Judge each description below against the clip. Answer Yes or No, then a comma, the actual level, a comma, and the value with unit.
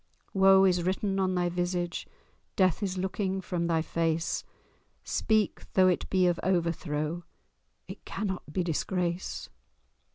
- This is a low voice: No, medium, 180 Hz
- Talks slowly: Yes, slow, 130 wpm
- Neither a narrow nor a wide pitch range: No, narrow, 1.9 semitones